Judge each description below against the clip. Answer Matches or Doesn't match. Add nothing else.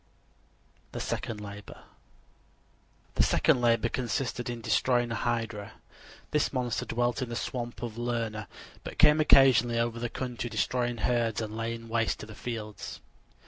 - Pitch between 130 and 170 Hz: Doesn't match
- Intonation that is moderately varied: Doesn't match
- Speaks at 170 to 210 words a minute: Doesn't match